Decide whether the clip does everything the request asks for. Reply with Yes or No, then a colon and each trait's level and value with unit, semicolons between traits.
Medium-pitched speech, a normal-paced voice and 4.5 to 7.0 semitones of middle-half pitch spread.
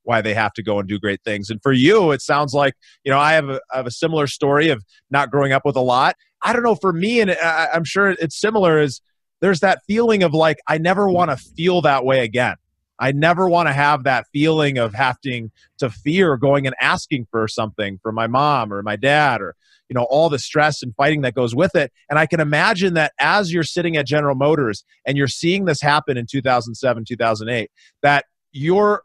No: medium, 145 Hz; fast, 230 wpm; average, 4.9 semitones